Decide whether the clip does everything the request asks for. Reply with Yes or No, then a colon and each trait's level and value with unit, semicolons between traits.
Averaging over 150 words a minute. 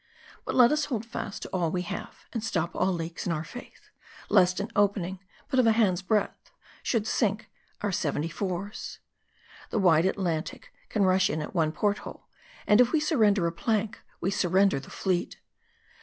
Yes: average, 185 wpm